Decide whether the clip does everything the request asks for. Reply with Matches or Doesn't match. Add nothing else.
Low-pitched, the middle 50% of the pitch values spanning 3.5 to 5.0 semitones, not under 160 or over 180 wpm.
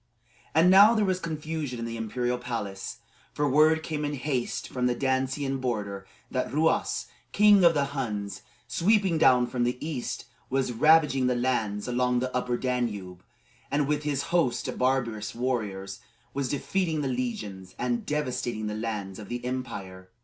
Matches